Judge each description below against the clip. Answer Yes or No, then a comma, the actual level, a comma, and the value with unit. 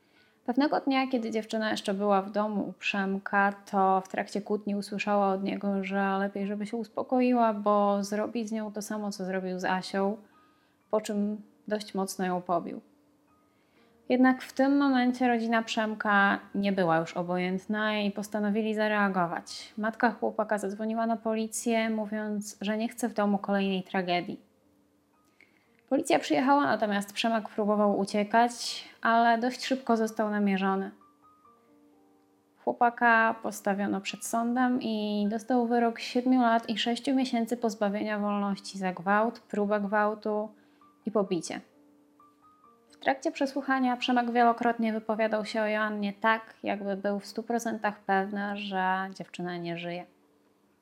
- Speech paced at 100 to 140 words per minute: Yes, average, 135 wpm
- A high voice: Yes, high, 215 Hz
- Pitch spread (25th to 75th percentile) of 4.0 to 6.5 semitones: No, average, 2.8 semitones